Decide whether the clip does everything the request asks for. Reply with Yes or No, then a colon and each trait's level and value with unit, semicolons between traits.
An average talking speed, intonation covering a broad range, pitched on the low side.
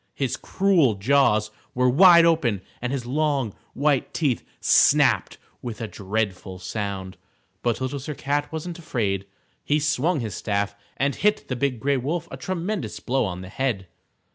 Yes: average, 160 wpm; wide, 6.0 semitones; low, 130 Hz